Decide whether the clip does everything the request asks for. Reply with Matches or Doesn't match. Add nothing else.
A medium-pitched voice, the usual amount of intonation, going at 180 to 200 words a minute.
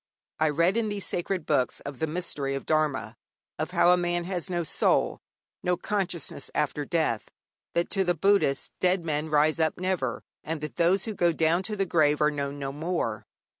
Matches